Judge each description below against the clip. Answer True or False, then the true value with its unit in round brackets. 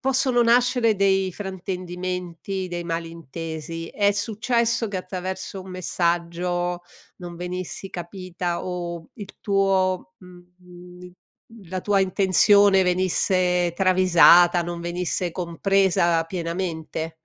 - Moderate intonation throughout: False (1.9 semitones)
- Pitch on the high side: False (180 Hz)